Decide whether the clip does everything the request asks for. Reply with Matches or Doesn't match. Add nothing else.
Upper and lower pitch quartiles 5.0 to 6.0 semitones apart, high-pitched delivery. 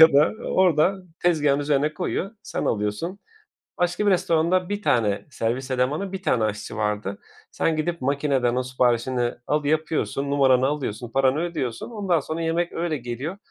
Doesn't match